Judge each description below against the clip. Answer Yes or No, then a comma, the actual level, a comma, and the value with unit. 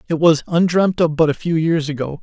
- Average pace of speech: No, fast, 240 wpm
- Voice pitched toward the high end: No, medium, 160 Hz